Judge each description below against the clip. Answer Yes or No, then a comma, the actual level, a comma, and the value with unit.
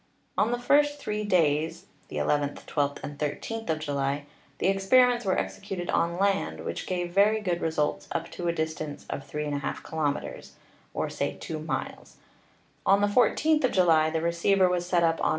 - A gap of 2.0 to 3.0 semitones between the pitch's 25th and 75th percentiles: No, average, 4.4 semitones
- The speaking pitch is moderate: Yes, medium, 175 Hz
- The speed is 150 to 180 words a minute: Yes, average, 175 wpm